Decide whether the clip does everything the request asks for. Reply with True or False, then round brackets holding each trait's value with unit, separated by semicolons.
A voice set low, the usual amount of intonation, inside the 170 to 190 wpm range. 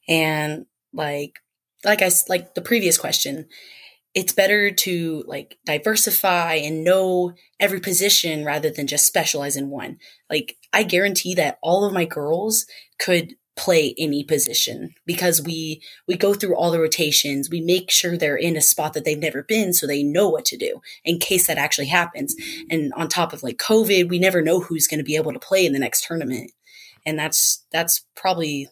False (170 Hz; 3.5 semitones; 185 wpm)